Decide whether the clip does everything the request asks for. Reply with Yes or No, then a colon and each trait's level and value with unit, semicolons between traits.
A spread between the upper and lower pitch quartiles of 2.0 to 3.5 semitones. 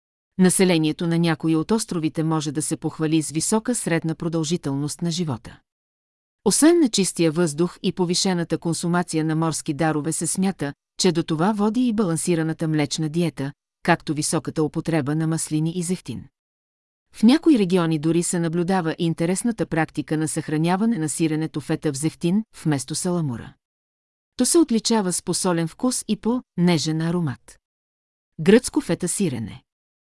Yes: average, 2.7 semitones